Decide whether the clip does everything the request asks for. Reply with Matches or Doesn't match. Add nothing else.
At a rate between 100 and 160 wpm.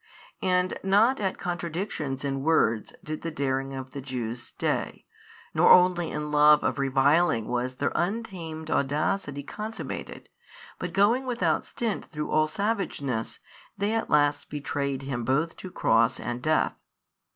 Matches